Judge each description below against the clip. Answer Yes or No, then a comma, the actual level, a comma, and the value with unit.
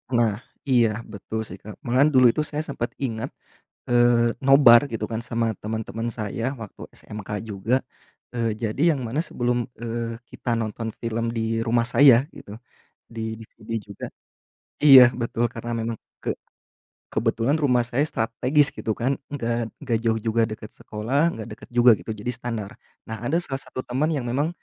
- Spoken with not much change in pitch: Yes, narrow, 2.2 semitones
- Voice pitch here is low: Yes, low, 115 Hz